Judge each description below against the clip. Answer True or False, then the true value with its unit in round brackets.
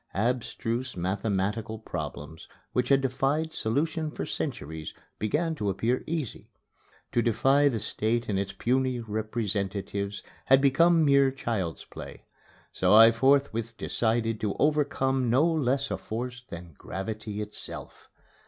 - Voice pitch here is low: True (115 Hz)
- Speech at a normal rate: False (125 wpm)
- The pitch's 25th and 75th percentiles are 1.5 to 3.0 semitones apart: False (4.4 semitones)